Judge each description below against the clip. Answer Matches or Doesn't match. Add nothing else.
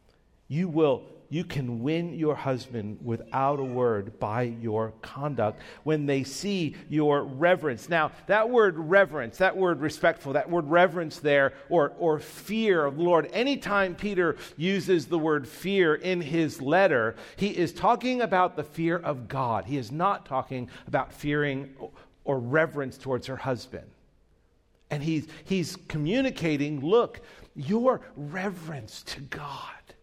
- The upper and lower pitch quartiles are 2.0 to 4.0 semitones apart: Doesn't match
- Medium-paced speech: Matches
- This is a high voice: Doesn't match